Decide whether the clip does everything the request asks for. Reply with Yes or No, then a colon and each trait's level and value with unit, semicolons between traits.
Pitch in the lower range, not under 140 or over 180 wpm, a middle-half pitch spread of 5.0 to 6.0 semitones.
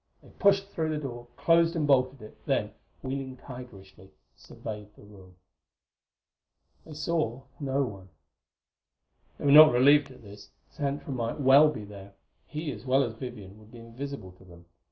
Yes: low, 130 Hz; average, 160 wpm; wide, 5.5 semitones